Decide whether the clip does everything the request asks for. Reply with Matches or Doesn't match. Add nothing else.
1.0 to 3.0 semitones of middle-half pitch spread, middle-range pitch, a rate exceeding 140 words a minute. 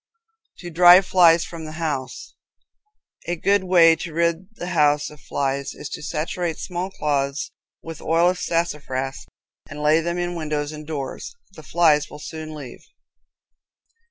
Matches